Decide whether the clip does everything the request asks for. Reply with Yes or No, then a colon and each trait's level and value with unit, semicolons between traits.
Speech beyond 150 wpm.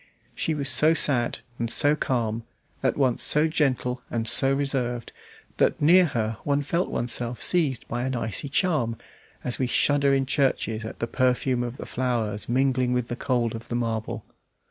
Yes: average, 175 wpm